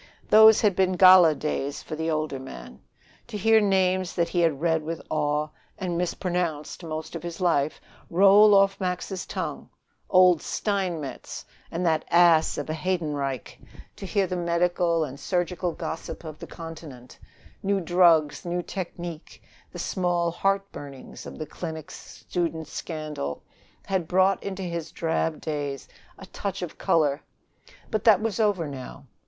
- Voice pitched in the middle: Yes, medium, 170 Hz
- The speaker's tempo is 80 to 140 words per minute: No, average, 150 wpm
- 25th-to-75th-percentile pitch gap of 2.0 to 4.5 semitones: Yes, average, 3.1 semitones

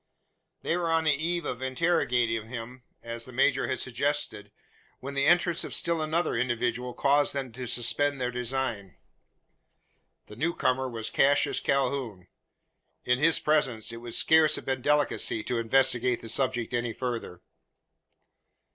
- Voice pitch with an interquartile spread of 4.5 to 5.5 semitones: No, average, 3.5 semitones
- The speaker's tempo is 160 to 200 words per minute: No, average, 150 wpm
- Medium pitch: No, low, 130 Hz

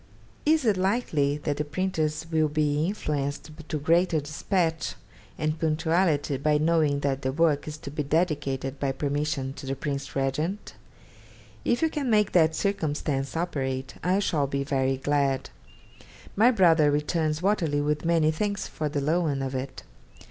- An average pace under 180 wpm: Yes, average, 155 wpm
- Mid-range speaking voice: Yes, medium, 150 Hz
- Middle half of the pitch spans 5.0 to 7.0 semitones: No, average, 3.0 semitones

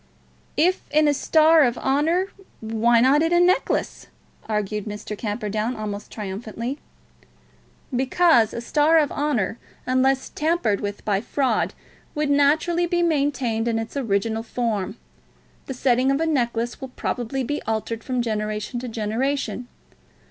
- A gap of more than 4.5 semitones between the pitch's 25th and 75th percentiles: Yes, average, 4.9 semitones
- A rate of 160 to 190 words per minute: No, average, 140 wpm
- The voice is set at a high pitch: Yes, high, 245 Hz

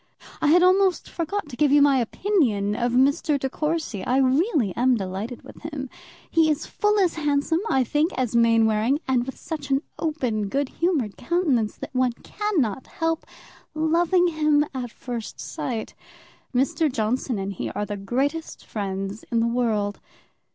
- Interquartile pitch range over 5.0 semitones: Yes, wide, 5.6 semitones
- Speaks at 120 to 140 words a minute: No, average, 165 wpm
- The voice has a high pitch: Yes, very high, 265 Hz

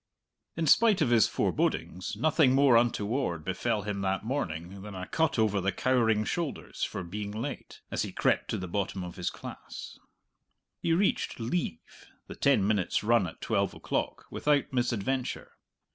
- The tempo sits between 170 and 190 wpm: No, average, 160 wpm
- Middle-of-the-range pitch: No, low, 110 Hz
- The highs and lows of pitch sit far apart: Yes, wide, 5.7 semitones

